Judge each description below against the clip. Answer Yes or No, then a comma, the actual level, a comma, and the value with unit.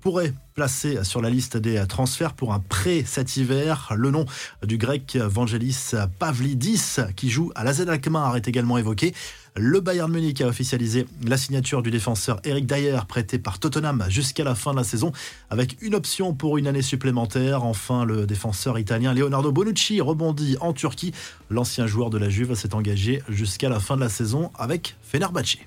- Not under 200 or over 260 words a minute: No, average, 180 wpm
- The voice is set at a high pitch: No, low, 130 Hz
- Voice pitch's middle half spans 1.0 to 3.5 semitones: No, average, 4.1 semitones